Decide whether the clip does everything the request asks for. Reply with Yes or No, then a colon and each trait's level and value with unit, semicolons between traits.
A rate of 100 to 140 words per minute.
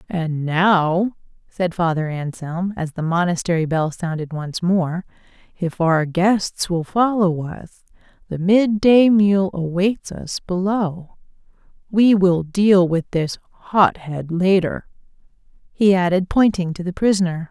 Yes: slow, 135 wpm